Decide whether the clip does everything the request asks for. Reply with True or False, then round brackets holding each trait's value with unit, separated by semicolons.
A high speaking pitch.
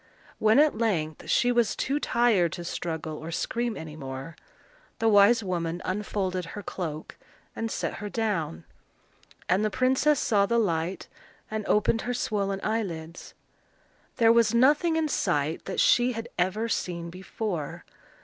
True (205 Hz)